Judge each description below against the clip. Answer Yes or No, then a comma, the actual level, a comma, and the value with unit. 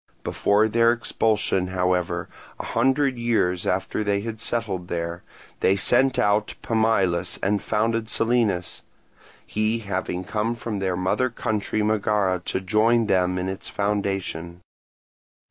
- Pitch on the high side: No, low, 105 Hz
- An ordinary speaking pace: No, slow, 130 wpm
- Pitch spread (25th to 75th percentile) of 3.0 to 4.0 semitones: Yes, average, 3.6 semitones